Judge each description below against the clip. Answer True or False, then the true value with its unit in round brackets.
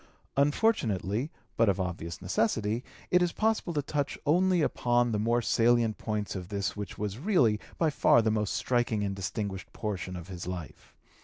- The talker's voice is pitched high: False (110 Hz)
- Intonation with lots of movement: True (6.1 semitones)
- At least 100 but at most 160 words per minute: False (170 wpm)